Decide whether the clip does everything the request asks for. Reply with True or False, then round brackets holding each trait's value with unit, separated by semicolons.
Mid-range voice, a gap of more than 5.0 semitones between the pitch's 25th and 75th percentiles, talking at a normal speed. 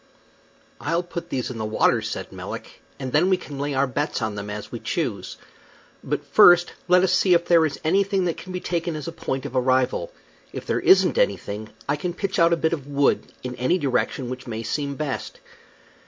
False (150 Hz; 5.4 semitones; 215 wpm)